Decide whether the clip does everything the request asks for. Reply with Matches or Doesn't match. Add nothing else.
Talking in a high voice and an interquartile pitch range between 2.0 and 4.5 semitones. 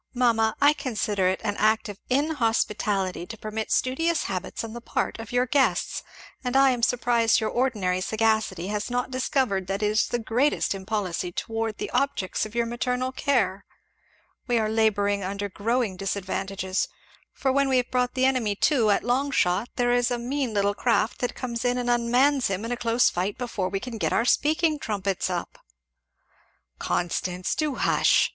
Matches